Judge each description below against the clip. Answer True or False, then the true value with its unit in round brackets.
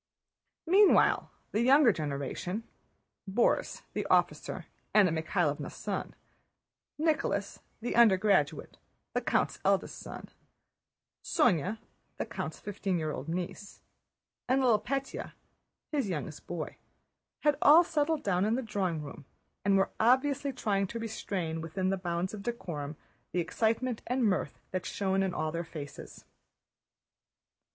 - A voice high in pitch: True (200 Hz)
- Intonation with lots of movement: True (6.1 semitones)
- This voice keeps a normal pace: False (130 wpm)